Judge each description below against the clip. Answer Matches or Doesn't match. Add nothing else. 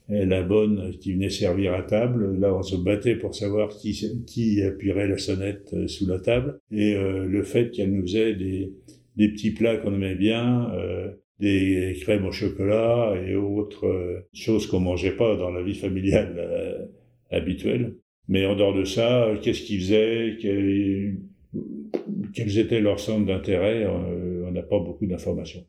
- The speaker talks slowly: Doesn't match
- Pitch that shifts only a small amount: Matches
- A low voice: Matches